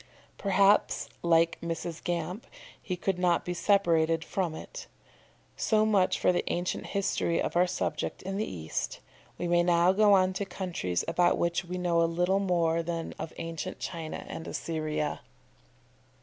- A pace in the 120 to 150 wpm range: No, average, 160 wpm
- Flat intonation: Yes, narrow, 2.2 semitones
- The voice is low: No, medium, 175 Hz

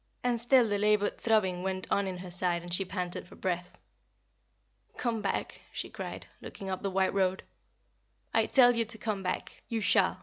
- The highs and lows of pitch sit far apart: No, average, 3.3 semitones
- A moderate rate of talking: Yes, average, 190 wpm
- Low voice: No, high, 195 Hz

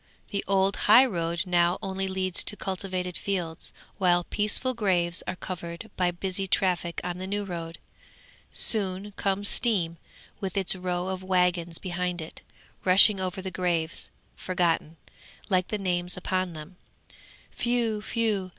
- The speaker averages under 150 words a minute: Yes, average, 140 wpm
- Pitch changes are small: Yes, narrow, 1.9 semitones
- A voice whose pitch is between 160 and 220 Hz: Yes, medium, 185 Hz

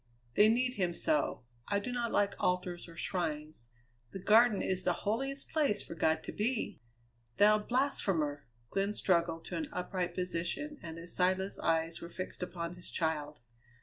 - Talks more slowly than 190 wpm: Yes, average, 165 wpm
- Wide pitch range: No, average, 4.2 semitones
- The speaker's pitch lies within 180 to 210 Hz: Yes, medium, 185 Hz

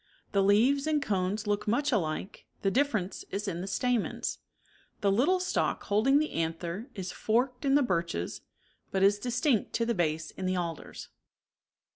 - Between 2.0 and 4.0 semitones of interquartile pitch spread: No, average, 5.3 semitones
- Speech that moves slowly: No, average, 175 wpm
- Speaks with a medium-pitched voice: No, high, 205 Hz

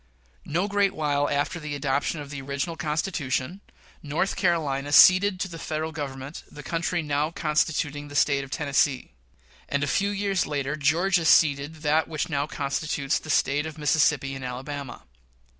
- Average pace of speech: Yes, average, 160 wpm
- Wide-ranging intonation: No, average, 2.7 semitones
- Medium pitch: Yes, medium, 150 Hz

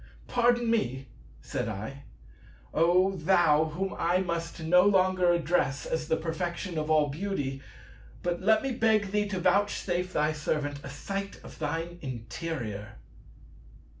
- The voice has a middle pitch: Yes, medium, 170 Hz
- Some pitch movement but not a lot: Yes, average, 4.2 semitones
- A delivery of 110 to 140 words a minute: Yes, slow, 135 wpm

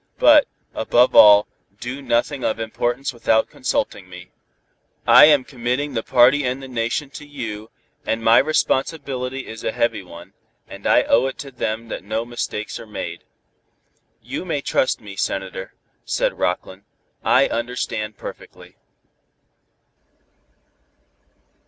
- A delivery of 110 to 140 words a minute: Yes, slow, 135 wpm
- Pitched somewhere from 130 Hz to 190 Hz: No, low, 120 Hz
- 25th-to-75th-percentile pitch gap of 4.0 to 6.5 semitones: No, average, 3.6 semitones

